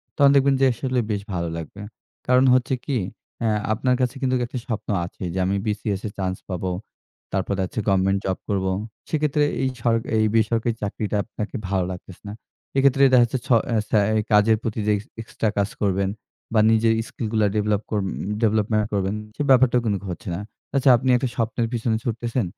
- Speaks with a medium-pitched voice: No, low, 110 Hz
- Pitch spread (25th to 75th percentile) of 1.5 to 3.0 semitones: No, average, 3.8 semitones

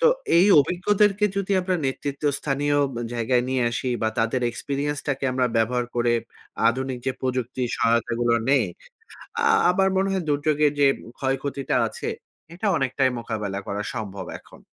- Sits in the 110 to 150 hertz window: Yes, low, 135 Hz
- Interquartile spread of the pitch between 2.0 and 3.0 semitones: No, average, 3.7 semitones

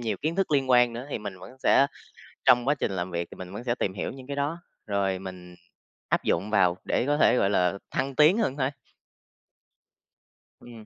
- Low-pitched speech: Yes, low, 120 Hz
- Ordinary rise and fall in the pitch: No, wide, 6.4 semitones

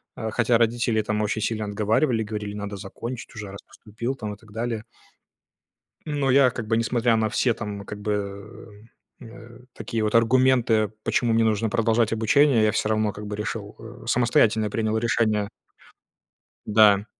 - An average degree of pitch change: No, narrow, 1.9 semitones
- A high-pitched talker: No, low, 110 Hz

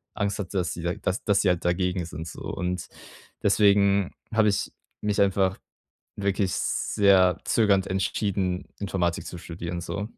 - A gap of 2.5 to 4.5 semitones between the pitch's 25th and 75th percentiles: No, narrow, 2.0 semitones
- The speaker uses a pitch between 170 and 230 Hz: No, very low, 95 Hz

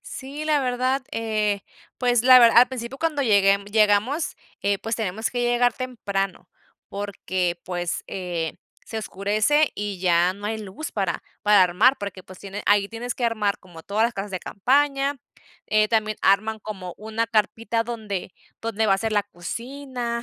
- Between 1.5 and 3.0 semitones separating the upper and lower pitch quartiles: No, average, 3.5 semitones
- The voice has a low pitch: No, high, 215 Hz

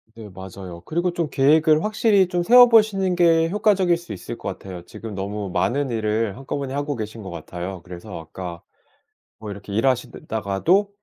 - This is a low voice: Yes, low, 130 Hz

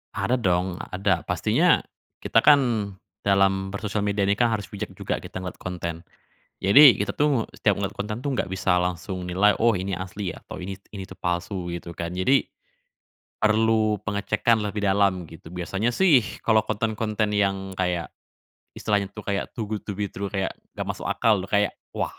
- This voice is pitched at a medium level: No, low, 100 Hz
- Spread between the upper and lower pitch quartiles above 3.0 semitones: No, average, 2.7 semitones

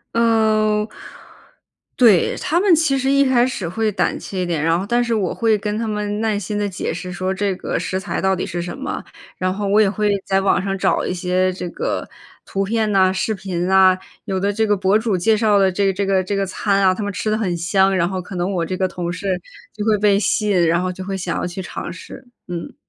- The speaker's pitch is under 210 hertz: Yes, high, 195 Hz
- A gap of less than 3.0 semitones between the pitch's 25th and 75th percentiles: Yes, narrow, 2.6 semitones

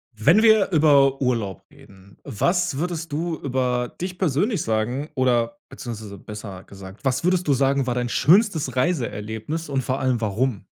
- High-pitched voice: No, low, 130 Hz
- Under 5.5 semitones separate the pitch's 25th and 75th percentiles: No, wide, 6.2 semitones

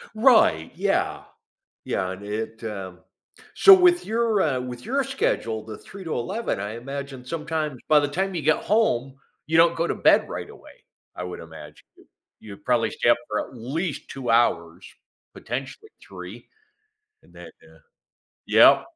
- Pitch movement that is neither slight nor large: No, wide, 7.9 semitones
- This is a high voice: No, low, 135 Hz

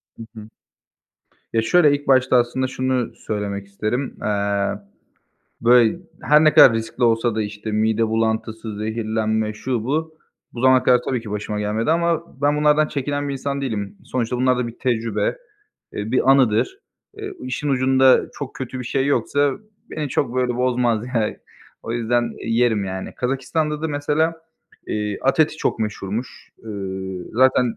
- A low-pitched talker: Yes, low, 120 Hz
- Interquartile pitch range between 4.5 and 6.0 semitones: No, average, 3.9 semitones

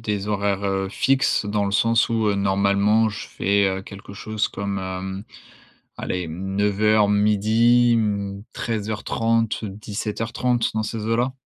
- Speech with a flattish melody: Yes, narrow, 2.1 semitones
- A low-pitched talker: Yes, low, 105 Hz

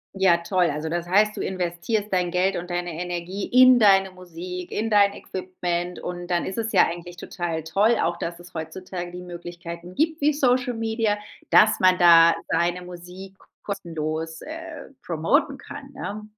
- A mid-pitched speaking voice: Yes, medium, 180 Hz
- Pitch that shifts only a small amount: No, average, 3.4 semitones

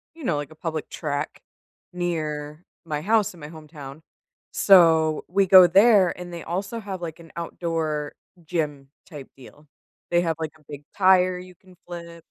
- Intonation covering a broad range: No, average, 3.0 semitones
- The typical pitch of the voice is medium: Yes, medium, 165 Hz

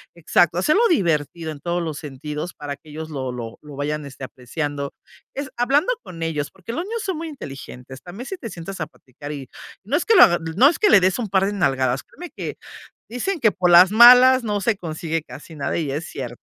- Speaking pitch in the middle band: Yes, medium, 170 Hz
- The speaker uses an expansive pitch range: Yes, wide, 8.5 semitones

